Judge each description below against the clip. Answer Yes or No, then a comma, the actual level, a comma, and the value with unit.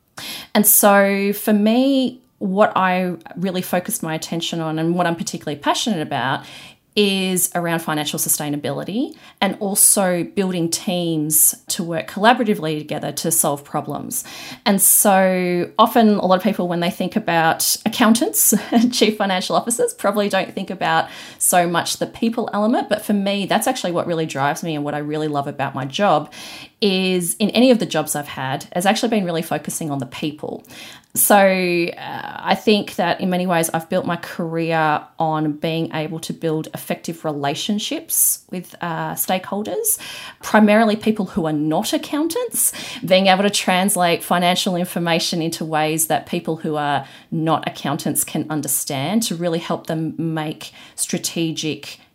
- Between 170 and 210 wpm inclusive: No, average, 160 wpm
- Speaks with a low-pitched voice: No, medium, 180 Hz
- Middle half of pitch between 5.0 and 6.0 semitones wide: No, average, 4.4 semitones